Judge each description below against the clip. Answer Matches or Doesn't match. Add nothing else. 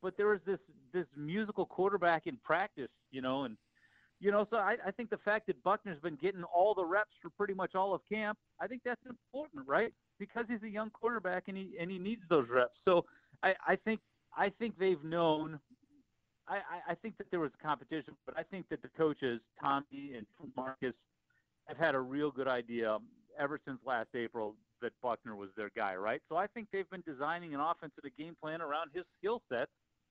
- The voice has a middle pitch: Matches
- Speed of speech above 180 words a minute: Matches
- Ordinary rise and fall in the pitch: Doesn't match